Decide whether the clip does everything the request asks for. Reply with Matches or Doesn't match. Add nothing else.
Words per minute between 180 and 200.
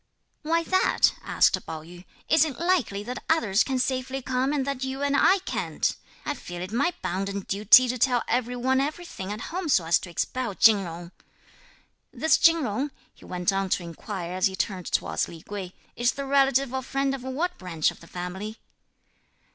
Matches